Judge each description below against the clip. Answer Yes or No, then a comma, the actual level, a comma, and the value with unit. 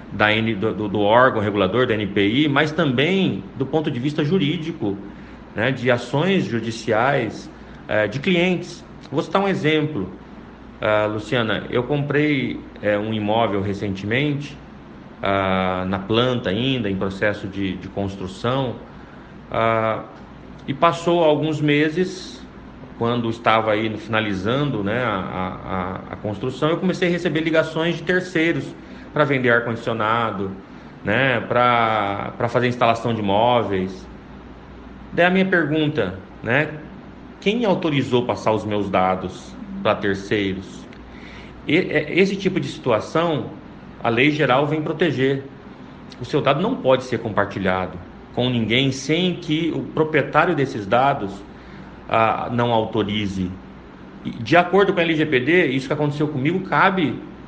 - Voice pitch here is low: Yes, low, 120 Hz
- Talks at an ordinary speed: Yes, average, 130 wpm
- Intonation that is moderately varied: No, wide, 6.9 semitones